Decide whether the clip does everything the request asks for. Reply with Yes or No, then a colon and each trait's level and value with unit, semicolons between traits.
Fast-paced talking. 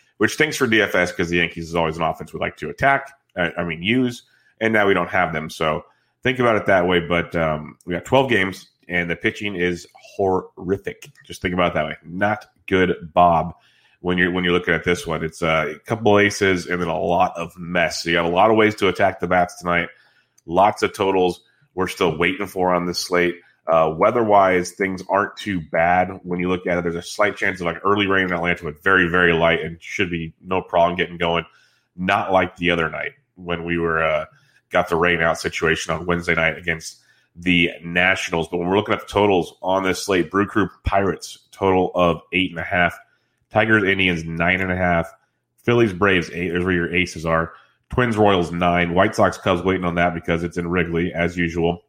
Yes: fast, 220 wpm